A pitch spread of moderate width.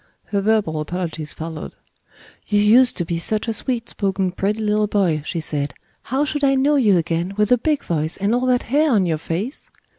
No: wide, 6.5 semitones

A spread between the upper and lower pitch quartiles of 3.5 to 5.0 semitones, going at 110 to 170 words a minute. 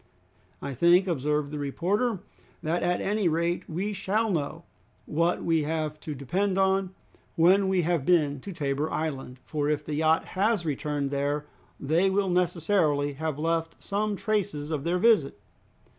Yes: average, 4.3 semitones; average, 160 wpm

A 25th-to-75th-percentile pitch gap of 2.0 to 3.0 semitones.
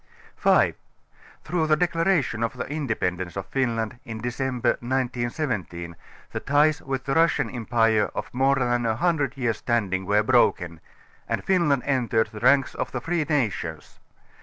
No: average, 4.3 semitones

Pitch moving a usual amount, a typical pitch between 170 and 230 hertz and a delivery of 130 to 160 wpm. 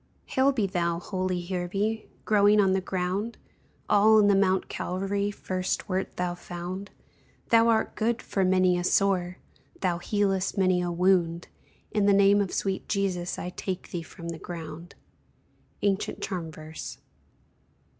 No: narrow, 2.3 semitones; high, 190 Hz; average, 150 wpm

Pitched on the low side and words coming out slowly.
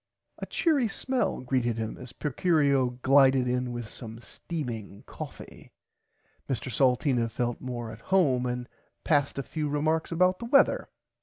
No: low, 130 Hz; average, 145 wpm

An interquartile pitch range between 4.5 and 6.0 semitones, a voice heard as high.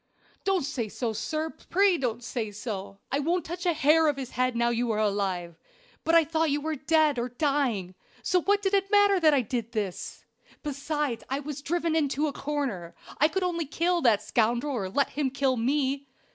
Yes: average, 5.2 semitones; very high, 280 Hz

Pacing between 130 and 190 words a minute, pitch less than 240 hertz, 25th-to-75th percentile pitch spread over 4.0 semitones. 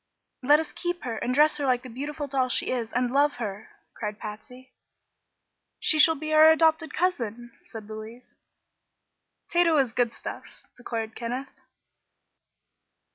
No: average, 145 wpm; very high, 255 Hz; average, 4.8 semitones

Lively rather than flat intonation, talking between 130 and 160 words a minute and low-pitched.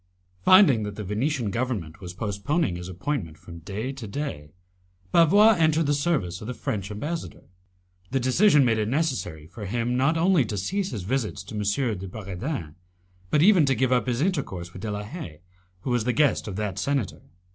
No: wide, 6.9 semitones; average, 190 wpm; low, 115 Hz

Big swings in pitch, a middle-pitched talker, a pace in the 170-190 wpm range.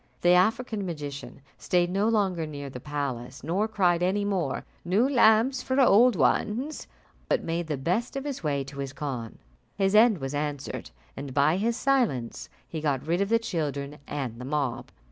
Yes: wide, 7.2 semitones; medium, 170 Hz; average, 180 wpm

